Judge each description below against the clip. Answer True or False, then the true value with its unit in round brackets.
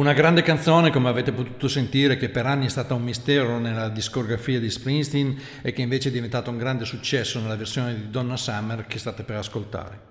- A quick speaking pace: True (210 wpm)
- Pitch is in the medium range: False (125 Hz)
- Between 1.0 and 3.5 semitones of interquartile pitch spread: True (3.0 semitones)